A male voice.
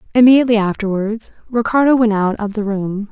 No: female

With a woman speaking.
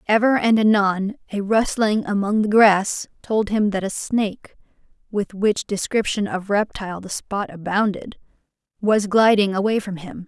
Yes: female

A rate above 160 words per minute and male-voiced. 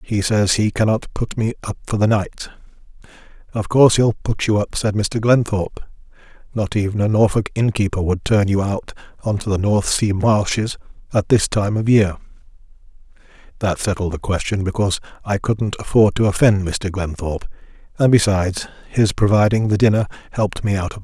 Yes: average, 180 wpm; male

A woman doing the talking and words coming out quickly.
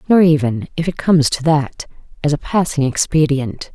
No: female; average, 175 wpm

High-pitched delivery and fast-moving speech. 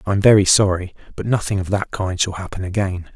No: very low, 95 Hz; fast, 210 wpm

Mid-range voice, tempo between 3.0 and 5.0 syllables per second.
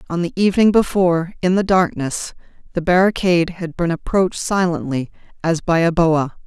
No: medium, 175 Hz; 5.4 syllables/s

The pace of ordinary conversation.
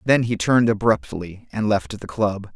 Yes: average, 190 wpm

